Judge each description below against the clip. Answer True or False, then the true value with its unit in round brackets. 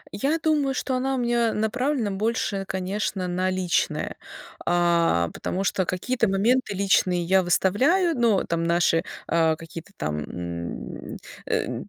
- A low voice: False (190 Hz)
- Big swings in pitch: True (5.7 semitones)